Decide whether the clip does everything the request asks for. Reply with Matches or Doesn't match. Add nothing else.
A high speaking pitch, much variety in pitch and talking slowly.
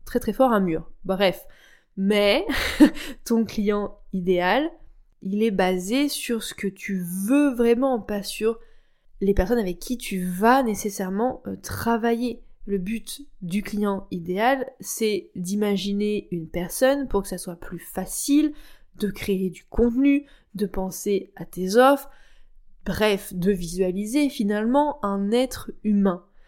Doesn't match